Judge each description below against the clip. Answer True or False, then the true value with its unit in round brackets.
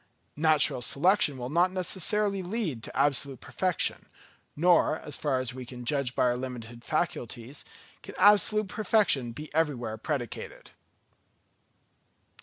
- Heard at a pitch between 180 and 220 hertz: False (145 Hz)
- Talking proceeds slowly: True (125 wpm)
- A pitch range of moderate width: False (6.5 semitones)